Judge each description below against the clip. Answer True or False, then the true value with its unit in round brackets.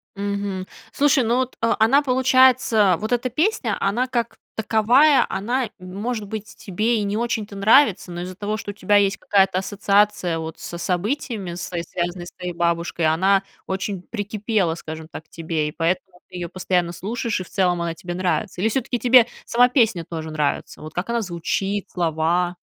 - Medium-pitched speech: False (200 Hz)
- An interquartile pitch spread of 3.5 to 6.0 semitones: True (4.6 semitones)